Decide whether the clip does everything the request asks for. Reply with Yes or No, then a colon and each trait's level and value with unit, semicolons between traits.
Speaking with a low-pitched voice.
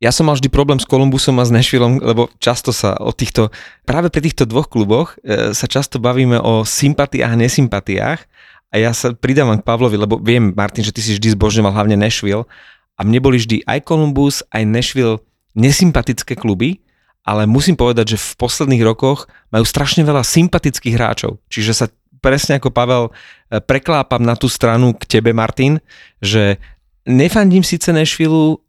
Yes: low, 125 Hz